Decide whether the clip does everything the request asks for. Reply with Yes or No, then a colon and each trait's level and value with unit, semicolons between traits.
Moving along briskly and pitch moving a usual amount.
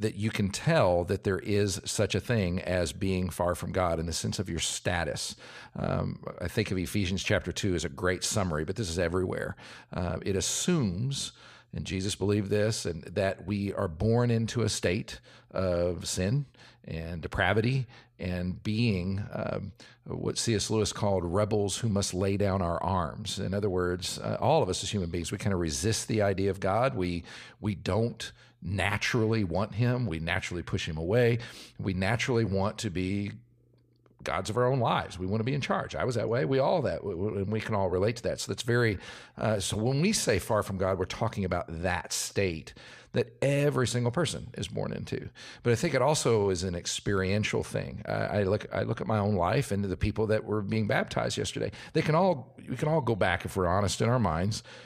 Yes: fast, 210 wpm; average, 3.5 semitones